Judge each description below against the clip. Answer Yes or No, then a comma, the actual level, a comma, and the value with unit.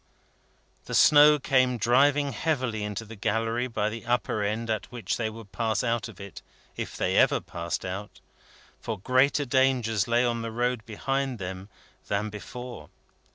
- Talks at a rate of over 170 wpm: No, average, 160 wpm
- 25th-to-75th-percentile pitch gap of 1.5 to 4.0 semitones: Yes, average, 3.0 semitones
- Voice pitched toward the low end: Yes, low, 115 Hz